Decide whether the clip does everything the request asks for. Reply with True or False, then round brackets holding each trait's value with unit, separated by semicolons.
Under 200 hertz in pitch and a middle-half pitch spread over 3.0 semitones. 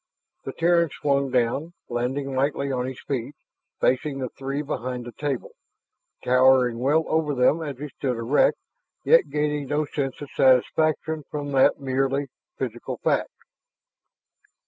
False (140 Hz; 2.5 semitones)